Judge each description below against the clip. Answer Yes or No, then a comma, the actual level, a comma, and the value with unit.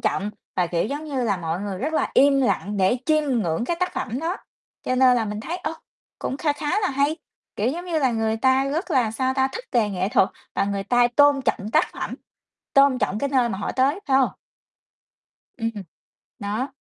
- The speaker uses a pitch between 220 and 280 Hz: Yes, very high, 255 Hz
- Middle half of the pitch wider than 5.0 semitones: Yes, wide, 5.4 semitones